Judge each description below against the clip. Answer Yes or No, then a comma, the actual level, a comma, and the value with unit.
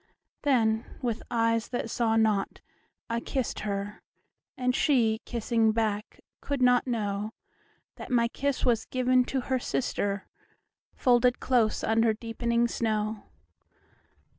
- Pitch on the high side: Yes, high, 230 Hz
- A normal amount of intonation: No, narrow, 2.2 semitones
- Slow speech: Yes, slow, 110 wpm